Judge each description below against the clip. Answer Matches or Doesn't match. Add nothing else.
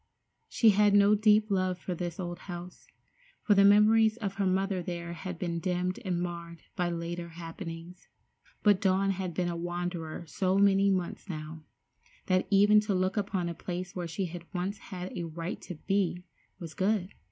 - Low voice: Doesn't match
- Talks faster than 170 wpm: Matches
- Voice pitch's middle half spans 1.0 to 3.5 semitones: Matches